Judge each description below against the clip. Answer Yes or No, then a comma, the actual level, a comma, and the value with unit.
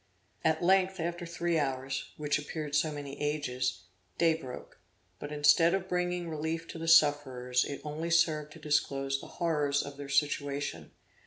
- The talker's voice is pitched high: No, medium, 150 Hz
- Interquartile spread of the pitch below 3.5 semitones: Yes, average, 2.8 semitones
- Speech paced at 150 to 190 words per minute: Yes, average, 160 wpm